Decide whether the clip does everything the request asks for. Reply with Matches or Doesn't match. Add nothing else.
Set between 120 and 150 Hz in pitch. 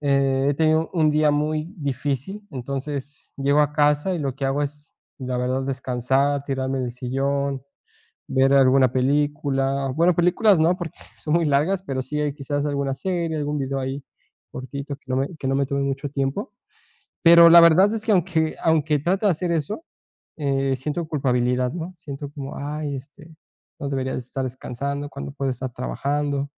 Matches